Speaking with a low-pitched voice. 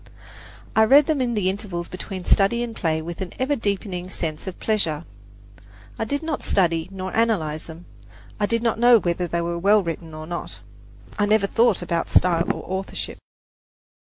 No: high, 190 Hz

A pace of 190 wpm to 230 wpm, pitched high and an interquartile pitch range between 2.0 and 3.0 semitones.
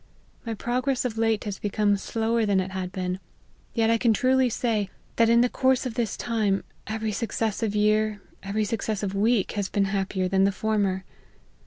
No: average, 180 wpm; high, 215 Hz; narrow, 2.6 semitones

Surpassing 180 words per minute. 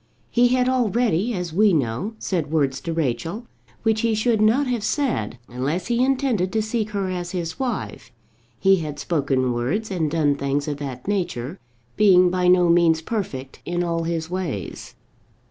No: average, 170 wpm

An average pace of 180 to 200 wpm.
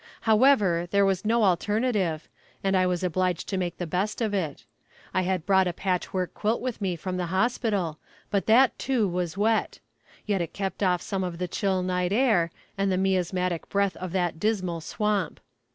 Yes: average, 190 wpm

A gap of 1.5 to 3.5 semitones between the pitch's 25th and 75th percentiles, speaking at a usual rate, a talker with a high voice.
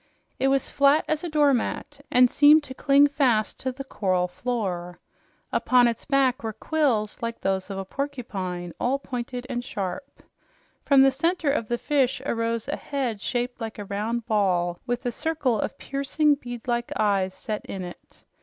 No: average, 4.8 semitones; average, 175 wpm; high, 245 Hz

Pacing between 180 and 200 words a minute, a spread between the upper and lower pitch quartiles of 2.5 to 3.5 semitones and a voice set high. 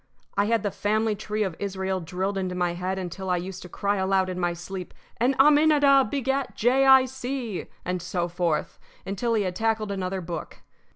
No: average, 190 wpm; average, 4.3 semitones; high, 195 Hz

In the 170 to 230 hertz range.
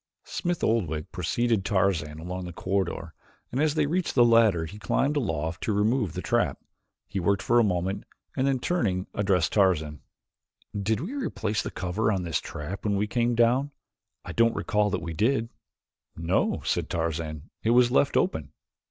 No: low, 100 Hz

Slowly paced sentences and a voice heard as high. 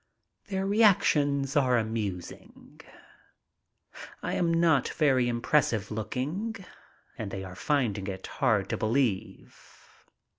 No: slow, 110 wpm; low, 130 Hz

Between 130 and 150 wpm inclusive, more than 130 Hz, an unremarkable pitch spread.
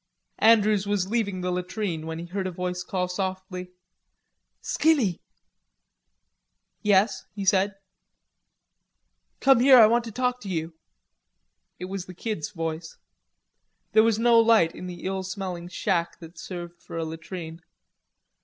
Yes: average, 140 wpm; medium, 185 Hz; average, 3.5 semitones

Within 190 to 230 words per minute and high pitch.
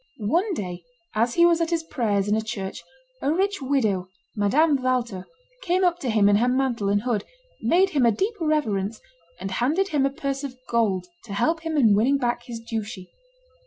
Yes: average, 200 wpm; high, 245 Hz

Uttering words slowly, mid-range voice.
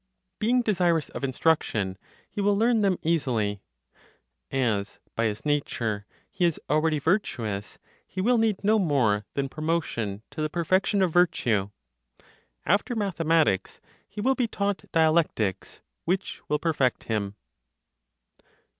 Yes: slow, 130 wpm; medium, 160 Hz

